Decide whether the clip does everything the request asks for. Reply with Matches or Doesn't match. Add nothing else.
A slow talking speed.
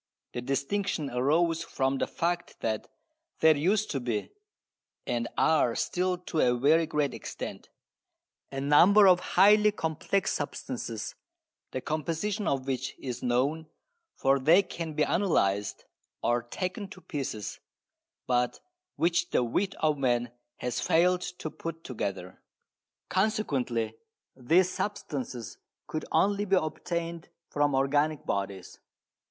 Matches